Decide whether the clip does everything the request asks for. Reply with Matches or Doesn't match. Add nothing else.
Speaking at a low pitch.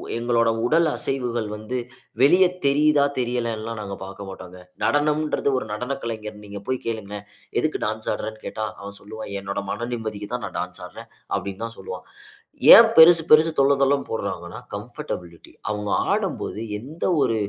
Matches